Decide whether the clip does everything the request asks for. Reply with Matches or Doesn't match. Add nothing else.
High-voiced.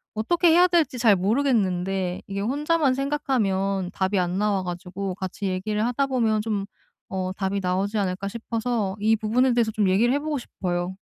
Matches